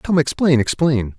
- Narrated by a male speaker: Yes, male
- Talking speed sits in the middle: Yes, average, 150 wpm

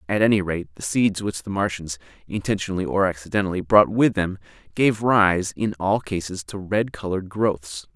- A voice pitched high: No, very low, 95 Hz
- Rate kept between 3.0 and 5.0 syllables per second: Yes, 4.1 syllables/s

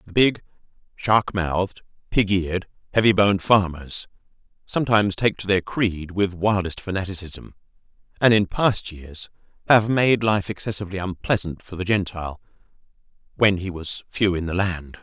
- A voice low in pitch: Yes, very low, 95 Hz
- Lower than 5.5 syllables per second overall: Yes, 5.0 syllables/s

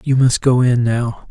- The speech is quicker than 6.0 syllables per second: No, 4.2 syllables/s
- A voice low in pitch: Yes, low, 125 Hz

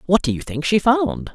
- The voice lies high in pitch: No, medium, 160 Hz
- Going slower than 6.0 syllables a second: Yes, 5.0 syllables/s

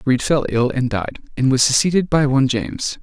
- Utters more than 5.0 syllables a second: Yes, 5.5 syllables/s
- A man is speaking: Yes, male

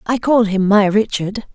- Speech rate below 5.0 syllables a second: Yes, 4.4 syllables/s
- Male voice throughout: No, female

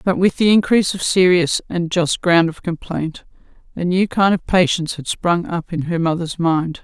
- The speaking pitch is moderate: Yes, medium, 175 Hz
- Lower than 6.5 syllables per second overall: Yes, 4.9 syllables/s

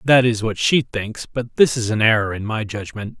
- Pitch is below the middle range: Yes, low, 115 Hz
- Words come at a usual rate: No, fast, 245 wpm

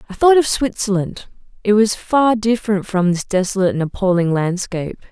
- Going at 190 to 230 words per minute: No, average, 165 wpm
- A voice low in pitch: No, high, 205 Hz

